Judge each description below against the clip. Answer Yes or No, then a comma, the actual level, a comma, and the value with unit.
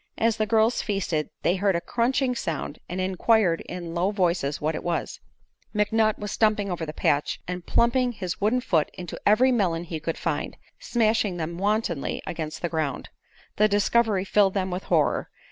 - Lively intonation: No, average, 4.3 semitones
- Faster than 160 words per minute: Yes, average, 180 wpm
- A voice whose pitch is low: No, high, 195 Hz